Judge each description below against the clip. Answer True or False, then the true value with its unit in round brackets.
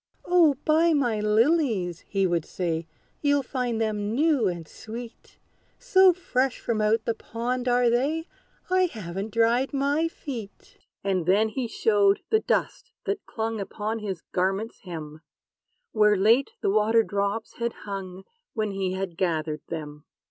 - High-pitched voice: True (220 Hz)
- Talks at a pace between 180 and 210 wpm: False (150 wpm)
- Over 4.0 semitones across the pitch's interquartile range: True (4.8 semitones)